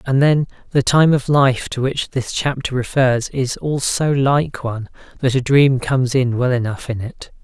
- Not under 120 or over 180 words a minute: No, average, 200 wpm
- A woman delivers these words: No, male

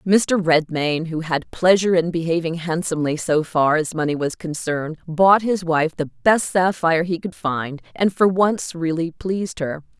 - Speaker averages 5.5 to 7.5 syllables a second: No, 4.6 syllables/s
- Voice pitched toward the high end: No, medium, 170 Hz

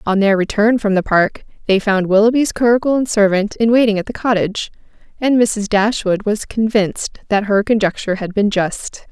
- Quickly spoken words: No, average, 185 wpm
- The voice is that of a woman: Yes, female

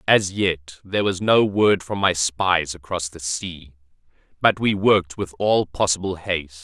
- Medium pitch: No, very low, 90 Hz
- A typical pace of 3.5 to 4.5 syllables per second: Yes, 4.4 syllables/s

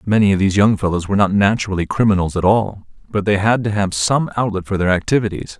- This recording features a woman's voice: No, male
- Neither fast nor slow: No, fast, 225 wpm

